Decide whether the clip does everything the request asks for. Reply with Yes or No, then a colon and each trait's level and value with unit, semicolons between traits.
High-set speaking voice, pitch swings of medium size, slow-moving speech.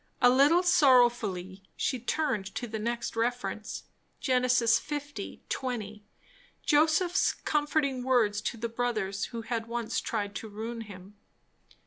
Yes: high, 235 Hz; average, 3.5 semitones; slow, 125 wpm